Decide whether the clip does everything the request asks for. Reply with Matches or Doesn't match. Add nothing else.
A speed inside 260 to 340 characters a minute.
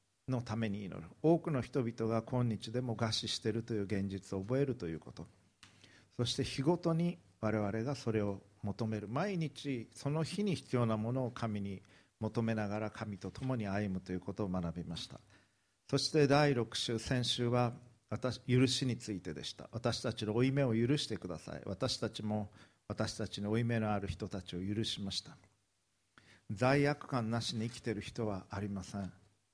Matches